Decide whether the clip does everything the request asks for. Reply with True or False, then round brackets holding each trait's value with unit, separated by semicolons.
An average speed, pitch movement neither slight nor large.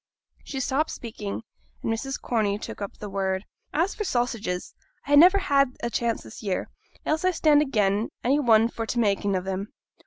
False (190 wpm; 5.8 semitones)